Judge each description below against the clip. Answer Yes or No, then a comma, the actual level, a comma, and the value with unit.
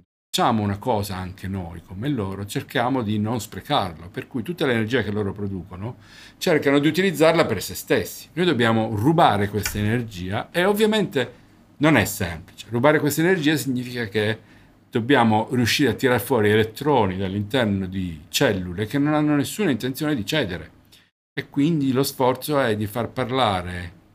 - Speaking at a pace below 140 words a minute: No, average, 155 wpm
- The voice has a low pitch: Yes, low, 115 Hz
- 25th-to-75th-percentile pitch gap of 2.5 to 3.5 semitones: No, wide, 5.5 semitones